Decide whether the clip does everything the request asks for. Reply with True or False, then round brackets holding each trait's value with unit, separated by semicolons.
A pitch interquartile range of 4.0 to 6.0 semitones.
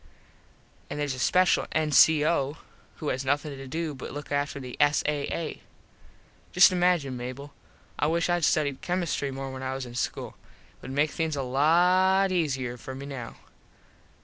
False (3.6 semitones)